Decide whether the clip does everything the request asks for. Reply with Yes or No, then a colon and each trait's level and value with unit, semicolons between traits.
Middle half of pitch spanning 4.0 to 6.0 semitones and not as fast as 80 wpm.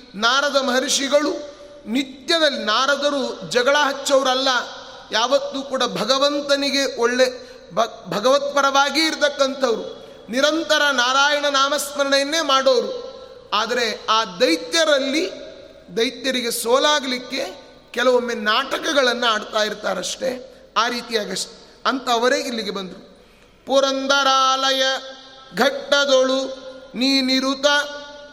No: narrow, 2.4 semitones; average, 70 wpm